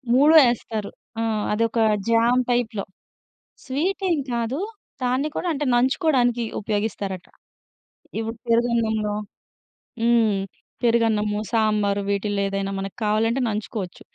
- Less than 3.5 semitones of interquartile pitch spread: Yes, average, 2.7 semitones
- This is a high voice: Yes, high, 230 Hz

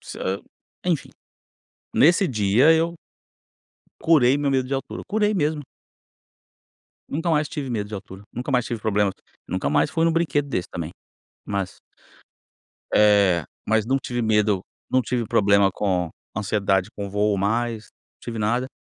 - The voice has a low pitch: Yes, low, 110 Hz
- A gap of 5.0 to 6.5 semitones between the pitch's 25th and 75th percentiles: Yes, wide, 5.6 semitones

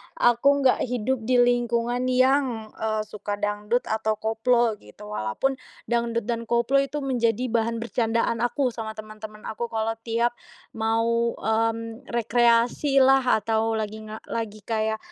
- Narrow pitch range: Yes, narrow, 1.8 semitones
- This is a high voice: Yes, high, 230 Hz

